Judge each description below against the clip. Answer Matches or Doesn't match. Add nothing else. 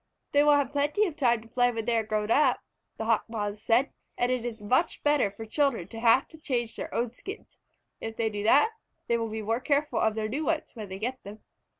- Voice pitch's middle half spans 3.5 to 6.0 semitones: Matches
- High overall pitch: Matches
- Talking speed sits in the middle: Doesn't match